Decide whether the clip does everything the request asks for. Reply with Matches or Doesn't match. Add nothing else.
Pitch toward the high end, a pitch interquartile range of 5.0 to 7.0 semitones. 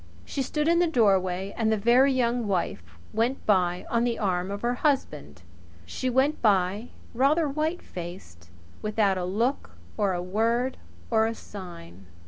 Matches